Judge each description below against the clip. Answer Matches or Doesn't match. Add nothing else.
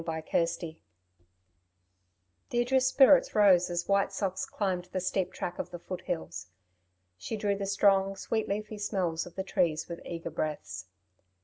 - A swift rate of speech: Doesn't match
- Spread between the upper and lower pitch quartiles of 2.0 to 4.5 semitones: Matches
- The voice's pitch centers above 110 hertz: Matches